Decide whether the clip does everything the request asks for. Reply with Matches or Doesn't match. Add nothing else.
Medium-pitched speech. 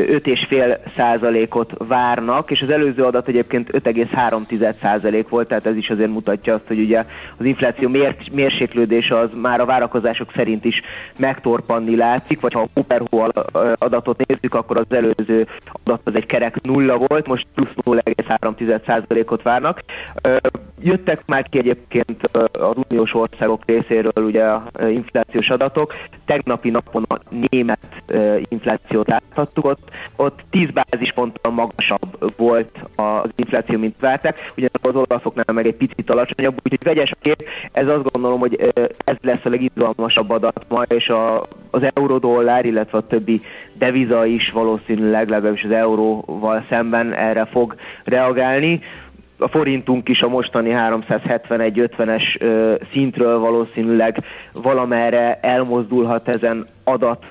Doesn't match